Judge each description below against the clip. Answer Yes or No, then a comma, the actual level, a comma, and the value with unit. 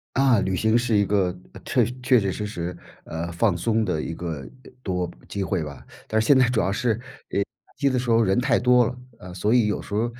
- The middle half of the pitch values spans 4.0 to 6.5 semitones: Yes, average, 5.0 semitones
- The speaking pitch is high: No, low, 105 Hz